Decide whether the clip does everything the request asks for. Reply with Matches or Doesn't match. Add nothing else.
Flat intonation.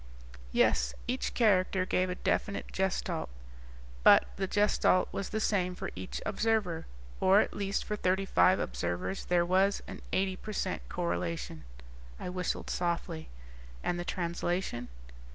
Matches